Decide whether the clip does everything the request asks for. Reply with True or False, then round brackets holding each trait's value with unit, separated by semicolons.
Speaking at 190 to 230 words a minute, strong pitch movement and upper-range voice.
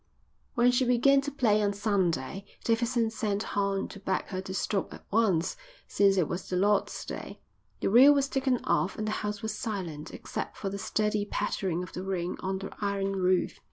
False (195 wpm; 2.9 semitones; 205 Hz)